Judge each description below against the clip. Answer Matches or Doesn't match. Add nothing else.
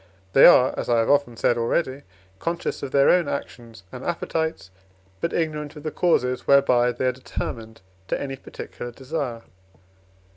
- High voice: Doesn't match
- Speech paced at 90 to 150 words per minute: Doesn't match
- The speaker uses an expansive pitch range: Doesn't match